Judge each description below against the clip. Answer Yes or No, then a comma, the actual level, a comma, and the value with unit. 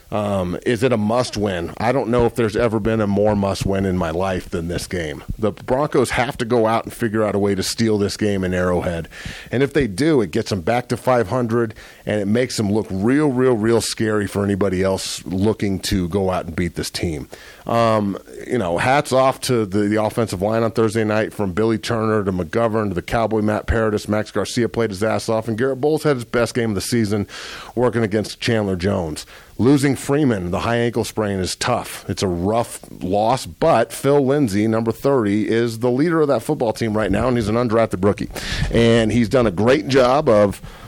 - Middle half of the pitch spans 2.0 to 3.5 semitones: Yes, average, 3.0 semitones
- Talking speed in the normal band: No, fast, 220 wpm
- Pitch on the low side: Yes, low, 110 Hz